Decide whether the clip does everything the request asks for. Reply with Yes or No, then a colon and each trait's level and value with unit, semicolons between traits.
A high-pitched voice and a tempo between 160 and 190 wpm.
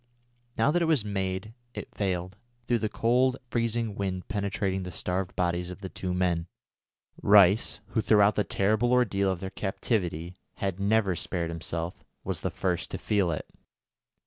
No: low, 100 Hz; average, 165 wpm